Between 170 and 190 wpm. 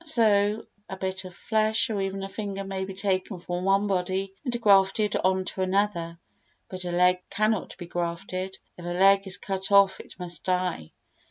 Yes: average, 185 wpm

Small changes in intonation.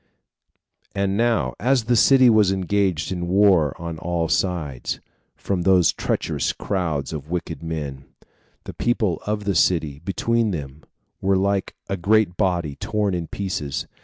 No: average, 3.9 semitones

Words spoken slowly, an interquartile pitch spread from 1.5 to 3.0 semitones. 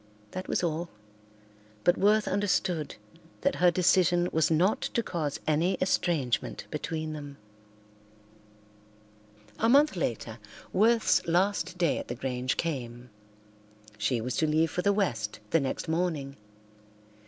No: slow, 130 wpm; average, 5.0 semitones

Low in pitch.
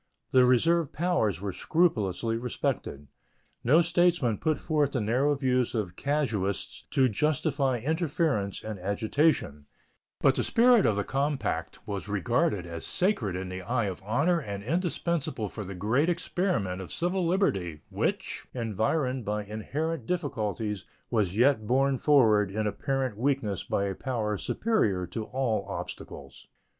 Yes: low, 120 Hz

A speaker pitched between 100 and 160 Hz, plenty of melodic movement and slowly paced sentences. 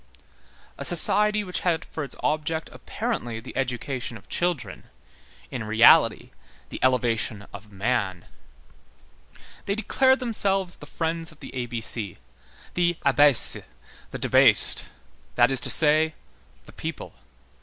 Yes: medium, 140 Hz; wide, 6.9 semitones; slow, 120 wpm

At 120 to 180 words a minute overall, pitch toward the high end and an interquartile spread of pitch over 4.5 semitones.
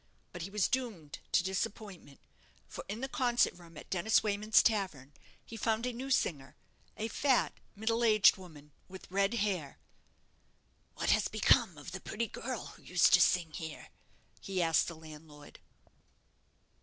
Yes: average, 155 wpm; high, 195 Hz; wide, 5.4 semitones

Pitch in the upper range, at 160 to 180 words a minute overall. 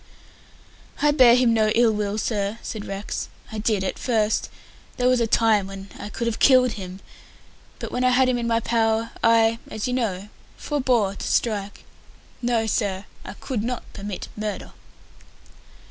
Yes: high, 225 Hz; average, 170 wpm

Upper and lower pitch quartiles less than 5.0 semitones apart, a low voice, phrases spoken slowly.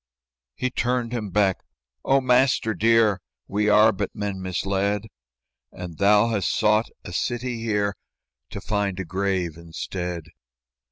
Yes: average, 3.2 semitones; low, 105 Hz; slow, 130 wpm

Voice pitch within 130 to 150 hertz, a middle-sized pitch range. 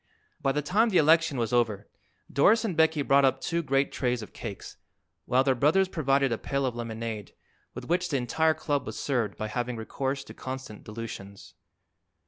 Yes: low, 135 Hz; average, 5.0 semitones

